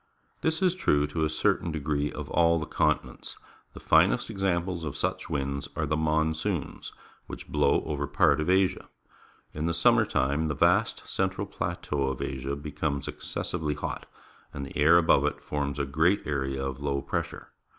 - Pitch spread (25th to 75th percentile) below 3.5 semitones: Yes, average, 3.0 semitones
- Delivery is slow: No, average, 170 wpm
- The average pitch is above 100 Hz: No, very low, 75 Hz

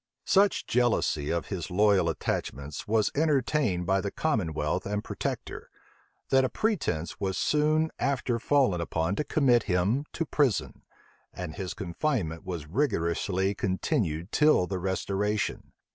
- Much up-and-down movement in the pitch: Yes, wide, 7.5 semitones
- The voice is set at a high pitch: No, low, 100 Hz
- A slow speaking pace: Yes, slow, 130 wpm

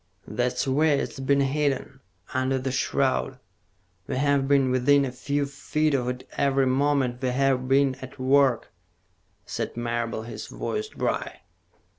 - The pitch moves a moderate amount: No, narrow, 1.7 semitones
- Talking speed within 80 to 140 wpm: Yes, slow, 135 wpm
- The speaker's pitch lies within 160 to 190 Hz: No, low, 135 Hz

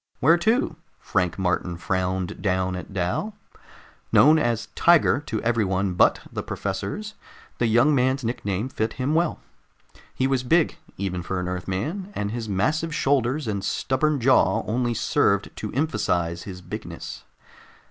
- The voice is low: Yes, low, 115 Hz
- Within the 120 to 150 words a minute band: Yes, average, 145 wpm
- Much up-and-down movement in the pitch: Yes, wide, 7.3 semitones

